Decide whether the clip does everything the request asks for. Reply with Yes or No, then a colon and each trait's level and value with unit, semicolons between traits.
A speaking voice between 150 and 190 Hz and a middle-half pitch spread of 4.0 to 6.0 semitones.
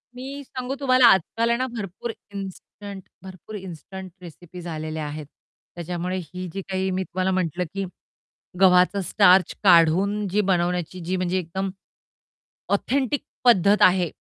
No: medium, 185 Hz; narrow, 2.4 semitones